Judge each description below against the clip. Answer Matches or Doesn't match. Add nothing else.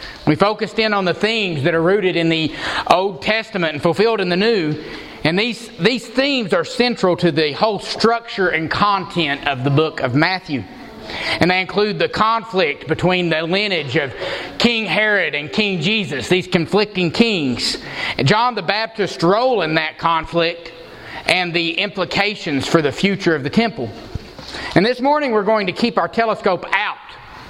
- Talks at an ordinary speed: Matches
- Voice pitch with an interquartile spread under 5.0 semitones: Matches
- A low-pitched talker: Doesn't match